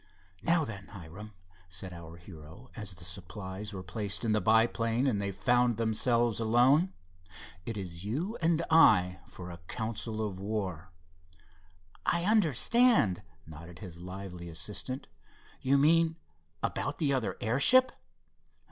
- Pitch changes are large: Yes, wide, 5.8 semitones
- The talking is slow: Yes, slow, 130 wpm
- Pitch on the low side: Yes, low, 110 Hz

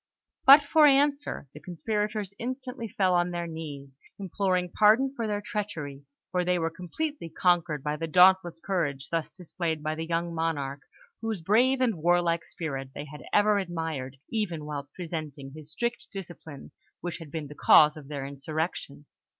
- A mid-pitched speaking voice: Yes, medium, 170 Hz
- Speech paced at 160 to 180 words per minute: Yes, average, 165 wpm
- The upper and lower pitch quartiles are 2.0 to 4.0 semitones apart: No, average, 5.2 semitones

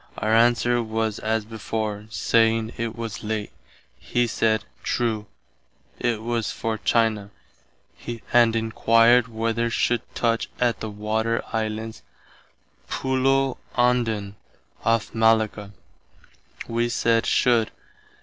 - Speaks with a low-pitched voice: Yes, low, 115 Hz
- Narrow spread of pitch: Yes, narrow, 1.2 semitones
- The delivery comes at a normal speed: No, slow, 105 wpm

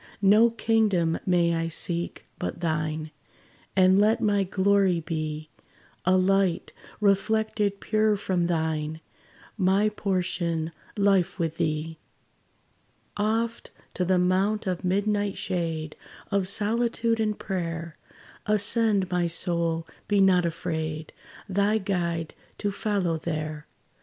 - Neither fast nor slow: No, slow, 110 wpm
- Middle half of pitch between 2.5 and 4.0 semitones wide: Yes, average, 3.6 semitones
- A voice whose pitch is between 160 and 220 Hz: Yes, medium, 185 Hz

